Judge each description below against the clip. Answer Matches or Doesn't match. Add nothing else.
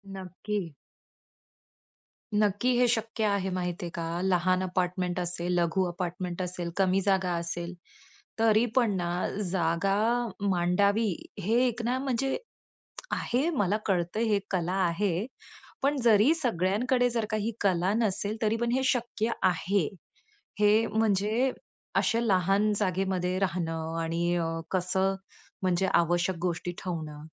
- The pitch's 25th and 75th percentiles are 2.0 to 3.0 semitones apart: Doesn't match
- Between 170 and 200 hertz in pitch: Matches